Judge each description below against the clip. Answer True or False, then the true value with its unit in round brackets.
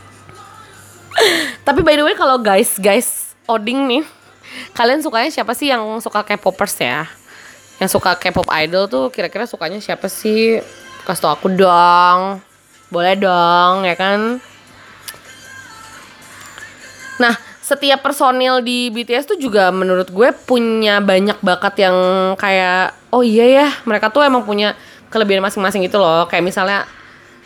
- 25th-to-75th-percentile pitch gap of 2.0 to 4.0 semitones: False (4.8 semitones)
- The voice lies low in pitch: False (205 Hz)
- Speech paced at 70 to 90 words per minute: False (135 wpm)